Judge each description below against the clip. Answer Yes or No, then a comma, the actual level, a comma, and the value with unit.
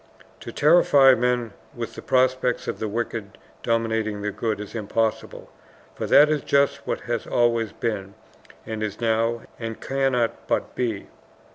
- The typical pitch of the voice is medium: No, low, 115 Hz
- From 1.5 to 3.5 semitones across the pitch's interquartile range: Yes, narrow, 2.4 semitones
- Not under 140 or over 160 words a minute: Yes, average, 150 wpm